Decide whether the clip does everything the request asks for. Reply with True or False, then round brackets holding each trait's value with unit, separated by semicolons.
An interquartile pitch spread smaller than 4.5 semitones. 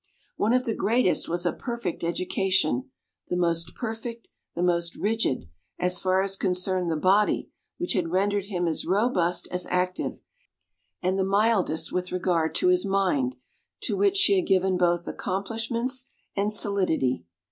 True (4.0 semitones)